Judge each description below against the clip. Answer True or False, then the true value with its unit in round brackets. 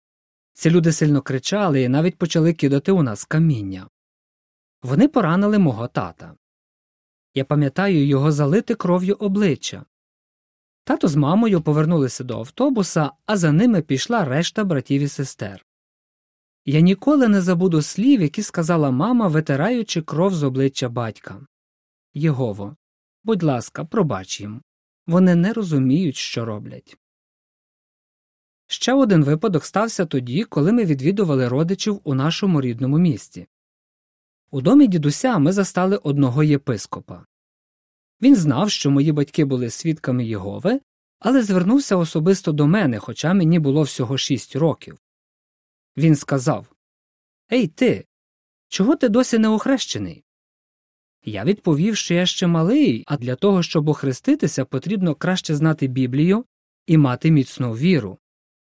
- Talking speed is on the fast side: False (130 wpm)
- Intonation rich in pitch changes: True (6.3 semitones)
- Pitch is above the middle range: False (160 Hz)